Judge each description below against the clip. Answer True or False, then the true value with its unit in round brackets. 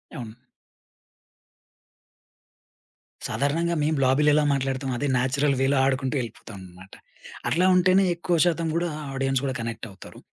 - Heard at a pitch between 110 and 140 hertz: True (135 Hz)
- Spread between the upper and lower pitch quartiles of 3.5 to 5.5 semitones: True (4.0 semitones)